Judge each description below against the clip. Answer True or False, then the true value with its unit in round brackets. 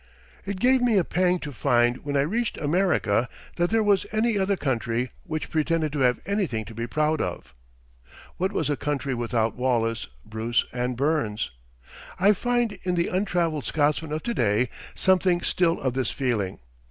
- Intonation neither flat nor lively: False (7.2 semitones)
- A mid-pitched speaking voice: True (150 Hz)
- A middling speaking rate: True (175 wpm)